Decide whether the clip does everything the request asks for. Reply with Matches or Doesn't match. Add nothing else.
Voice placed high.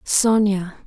Matches